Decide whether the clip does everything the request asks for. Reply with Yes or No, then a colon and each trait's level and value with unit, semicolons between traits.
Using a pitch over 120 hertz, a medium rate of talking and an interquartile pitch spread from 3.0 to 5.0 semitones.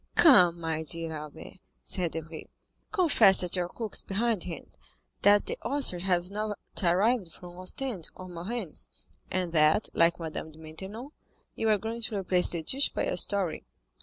Yes: medium, 185 Hz; average, 165 wpm; average, 4.5 semitones